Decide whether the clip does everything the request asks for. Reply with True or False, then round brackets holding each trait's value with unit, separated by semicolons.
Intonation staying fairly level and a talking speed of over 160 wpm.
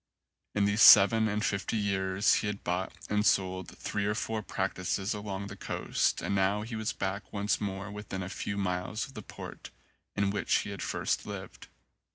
True (1.6 semitones; 190 wpm)